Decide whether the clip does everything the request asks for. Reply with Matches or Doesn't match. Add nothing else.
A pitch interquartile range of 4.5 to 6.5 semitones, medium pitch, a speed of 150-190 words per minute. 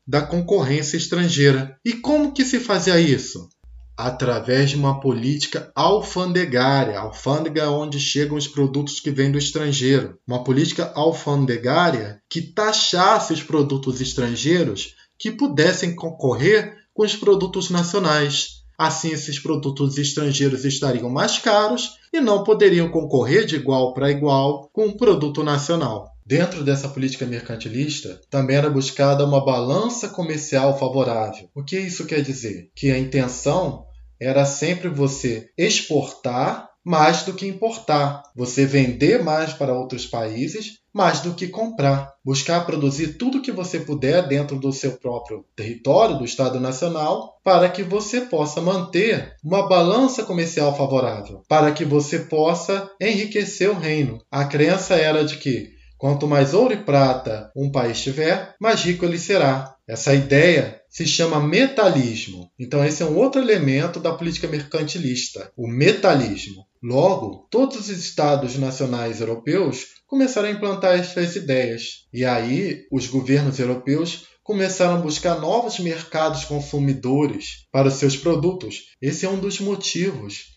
Doesn't match